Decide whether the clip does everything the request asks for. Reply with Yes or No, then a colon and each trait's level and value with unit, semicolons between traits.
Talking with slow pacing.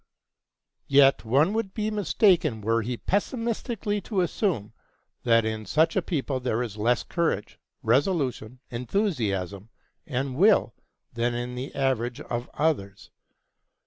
Yes: slow, 125 wpm